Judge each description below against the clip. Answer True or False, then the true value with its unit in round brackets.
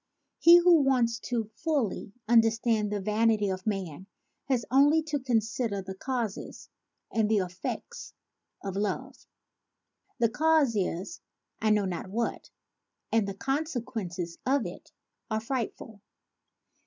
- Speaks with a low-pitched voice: False (225 Hz)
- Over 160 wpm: False (135 wpm)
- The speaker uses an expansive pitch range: False (4.7 semitones)